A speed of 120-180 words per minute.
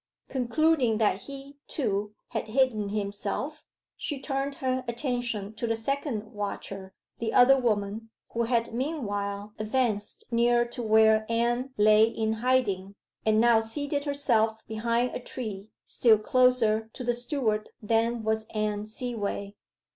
Yes: slow, 135 wpm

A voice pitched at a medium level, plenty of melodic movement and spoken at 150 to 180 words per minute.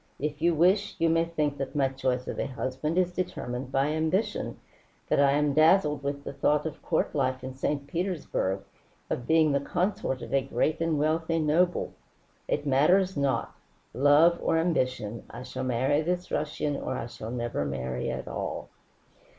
No: medium, 145 Hz; average, 3.9 semitones; average, 175 wpm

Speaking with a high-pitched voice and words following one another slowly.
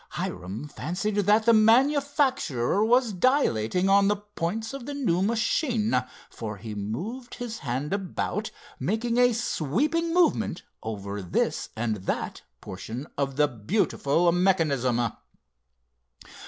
Yes: high, 195 Hz; slow, 120 wpm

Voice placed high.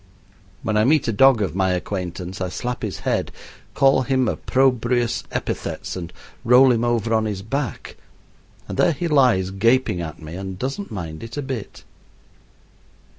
No: low, 115 Hz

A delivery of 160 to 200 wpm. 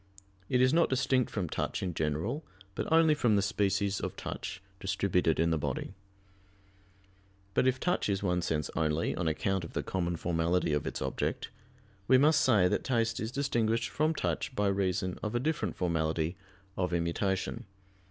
Yes: average, 170 wpm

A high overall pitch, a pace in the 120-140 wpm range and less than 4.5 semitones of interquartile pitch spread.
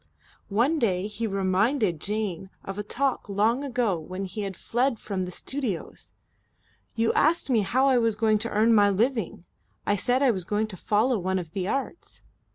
No: high, 215 Hz; average, 185 wpm; average, 4.0 semitones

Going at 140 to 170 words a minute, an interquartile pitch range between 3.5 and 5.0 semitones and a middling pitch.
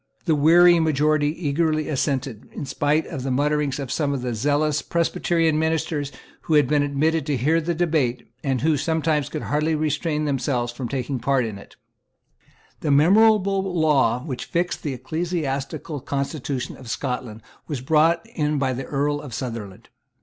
No: average, 155 wpm; average, 3.0 semitones; medium, 145 Hz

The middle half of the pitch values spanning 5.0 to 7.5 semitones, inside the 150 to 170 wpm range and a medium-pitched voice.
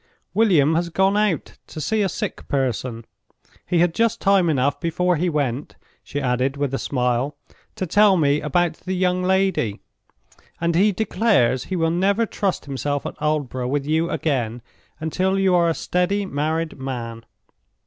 Yes: average, 5.3 semitones; average, 165 wpm; medium, 160 Hz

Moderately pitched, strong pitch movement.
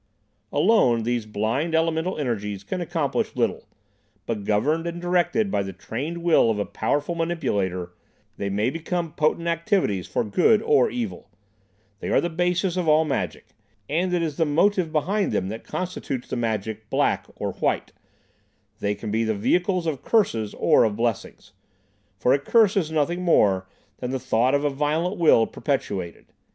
Yes: medium, 150 Hz; wide, 7.7 semitones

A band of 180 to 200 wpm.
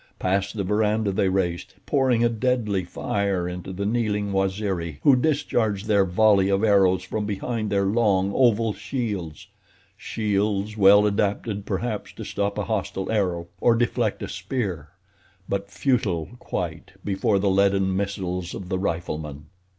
No: average, 145 wpm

